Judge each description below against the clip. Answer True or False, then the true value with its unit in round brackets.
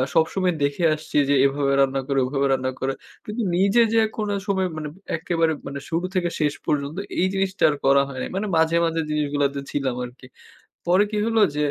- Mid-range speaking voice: True (155 Hz)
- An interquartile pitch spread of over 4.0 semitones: True (4.9 semitones)